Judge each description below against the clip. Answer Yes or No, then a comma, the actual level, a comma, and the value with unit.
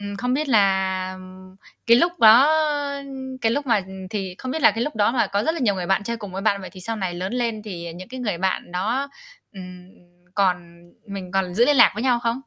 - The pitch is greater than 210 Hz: No, high, 205 Hz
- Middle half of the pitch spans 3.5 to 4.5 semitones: Yes, average, 4.2 semitones